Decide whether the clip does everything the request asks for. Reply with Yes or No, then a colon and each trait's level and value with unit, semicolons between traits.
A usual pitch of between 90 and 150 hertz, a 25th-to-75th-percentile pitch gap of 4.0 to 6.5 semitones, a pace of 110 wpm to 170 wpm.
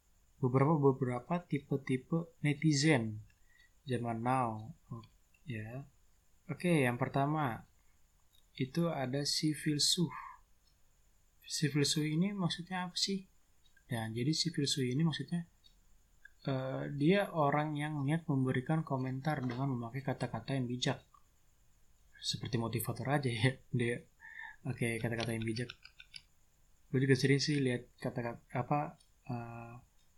Yes: low, 135 Hz; average, 4.3 semitones; average, 125 wpm